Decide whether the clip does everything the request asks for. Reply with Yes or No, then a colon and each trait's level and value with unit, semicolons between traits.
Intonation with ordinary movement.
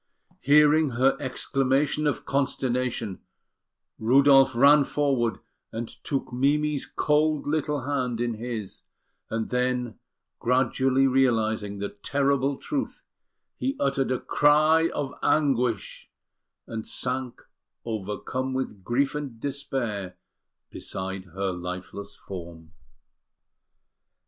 Yes: average, 4.1 semitones